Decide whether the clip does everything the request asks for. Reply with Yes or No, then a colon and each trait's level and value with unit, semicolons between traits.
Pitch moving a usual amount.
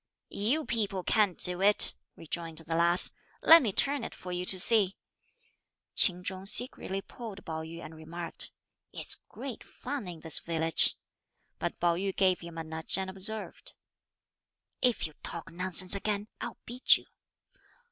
Yes: average, 3.8 semitones